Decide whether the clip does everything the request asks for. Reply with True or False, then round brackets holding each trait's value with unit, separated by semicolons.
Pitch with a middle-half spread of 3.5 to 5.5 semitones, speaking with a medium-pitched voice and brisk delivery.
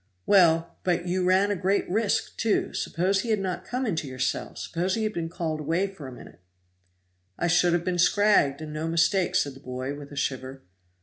True (4.2 semitones; 175 Hz; 210 wpm)